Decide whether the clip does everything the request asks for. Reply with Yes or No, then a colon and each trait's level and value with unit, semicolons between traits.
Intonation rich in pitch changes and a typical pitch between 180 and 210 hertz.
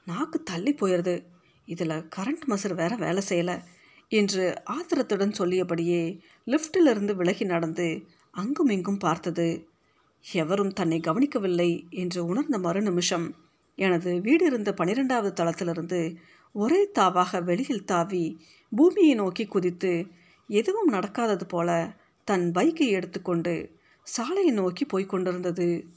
No: average, 3.8 semitones; medium, 185 Hz